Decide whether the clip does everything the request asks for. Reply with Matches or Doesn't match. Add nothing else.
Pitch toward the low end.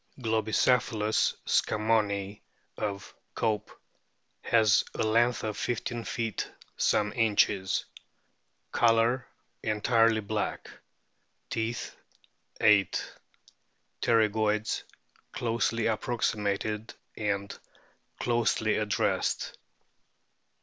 Matches